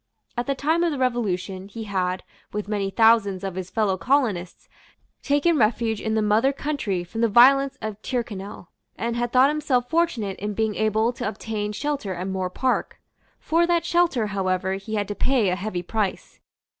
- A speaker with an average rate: Yes, average, 180 wpm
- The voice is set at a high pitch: Yes, high, 220 Hz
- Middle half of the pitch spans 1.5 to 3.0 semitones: No, average, 4.8 semitones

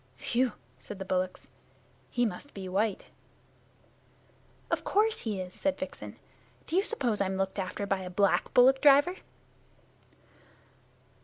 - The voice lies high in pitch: Yes, high, 210 Hz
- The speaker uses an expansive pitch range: Yes, wide, 6.6 semitones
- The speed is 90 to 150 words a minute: Yes, slow, 135 wpm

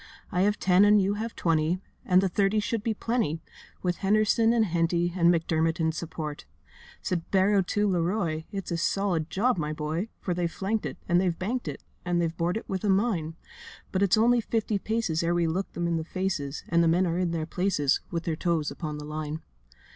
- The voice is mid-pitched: Yes, medium, 175 Hz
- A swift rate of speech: Yes, fast, 215 wpm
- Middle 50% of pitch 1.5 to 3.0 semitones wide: No, average, 3.6 semitones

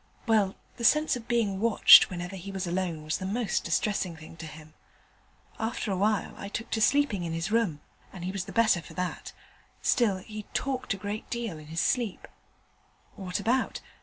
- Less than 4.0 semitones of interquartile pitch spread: No, average, 4.5 semitones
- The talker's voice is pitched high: Yes, high, 200 Hz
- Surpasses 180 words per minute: Yes, average, 195 wpm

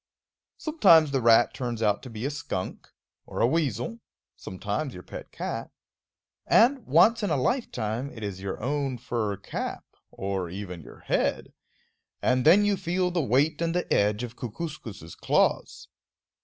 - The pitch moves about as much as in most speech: No, wide, 7.8 semitones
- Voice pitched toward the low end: Yes, low, 125 Hz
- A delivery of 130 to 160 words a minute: Yes, average, 155 wpm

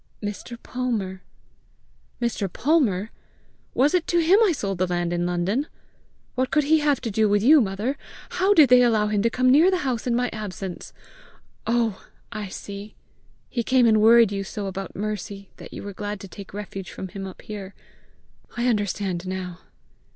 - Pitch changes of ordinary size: Yes, average, 4.4 semitones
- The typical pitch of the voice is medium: No, high, 215 Hz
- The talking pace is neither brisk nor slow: Yes, average, 180 wpm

